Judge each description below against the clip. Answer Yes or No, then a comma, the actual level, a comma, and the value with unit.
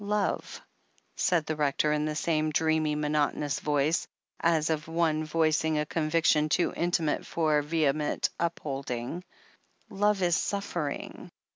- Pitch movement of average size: No, narrow, 1.8 semitones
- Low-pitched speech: No, medium, 155 Hz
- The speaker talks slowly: Yes, slow, 130 wpm